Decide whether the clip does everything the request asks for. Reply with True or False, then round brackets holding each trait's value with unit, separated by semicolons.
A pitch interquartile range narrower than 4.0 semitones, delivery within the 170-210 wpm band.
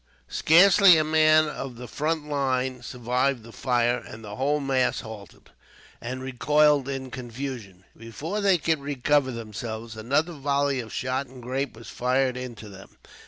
False (3.5 semitones; 155 wpm)